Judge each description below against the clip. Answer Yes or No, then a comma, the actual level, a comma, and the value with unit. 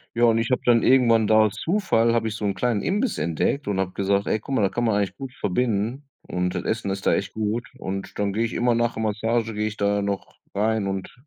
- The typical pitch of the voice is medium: No, low, 110 Hz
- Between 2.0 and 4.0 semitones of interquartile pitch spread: Yes, average, 2.8 semitones